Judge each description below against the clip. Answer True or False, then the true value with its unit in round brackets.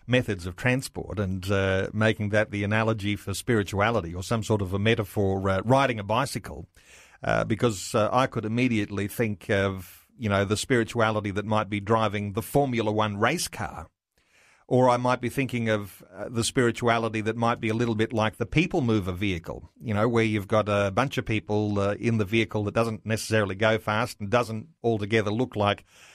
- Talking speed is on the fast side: False (195 wpm)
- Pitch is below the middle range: True (110 Hz)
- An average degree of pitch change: False (2.3 semitones)